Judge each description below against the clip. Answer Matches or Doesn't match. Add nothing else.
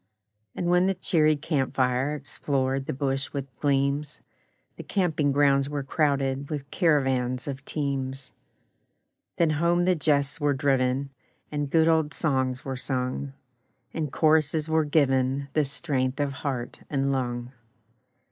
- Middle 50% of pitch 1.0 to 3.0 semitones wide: Matches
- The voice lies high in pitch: Doesn't match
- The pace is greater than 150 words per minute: Doesn't match